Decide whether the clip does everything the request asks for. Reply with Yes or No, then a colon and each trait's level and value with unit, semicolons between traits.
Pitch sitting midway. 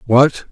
No: low, 130 Hz